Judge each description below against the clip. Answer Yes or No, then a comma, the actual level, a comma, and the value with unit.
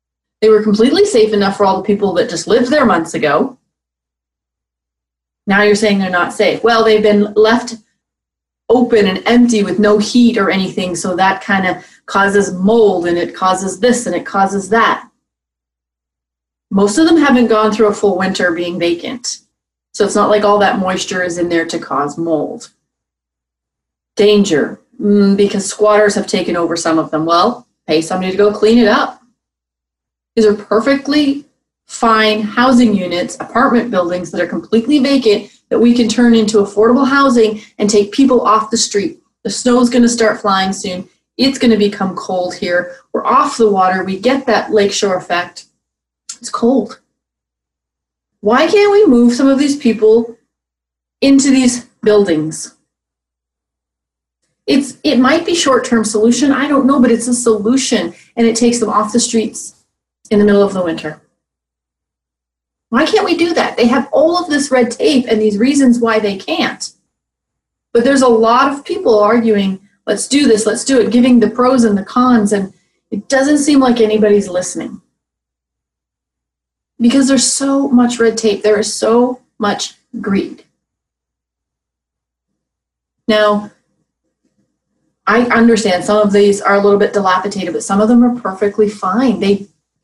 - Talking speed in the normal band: Yes, average, 165 wpm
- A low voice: No, high, 210 Hz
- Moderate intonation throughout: Yes, average, 5.0 semitones